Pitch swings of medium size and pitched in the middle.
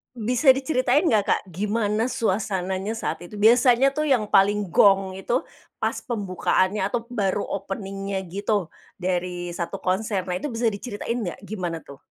No: average, 3.6 semitones; high, 205 Hz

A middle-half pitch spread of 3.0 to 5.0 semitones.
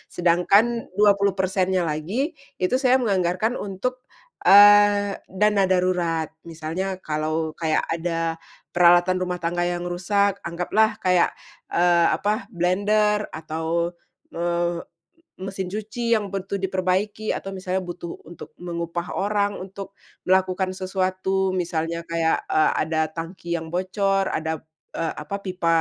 No: narrow, 2.6 semitones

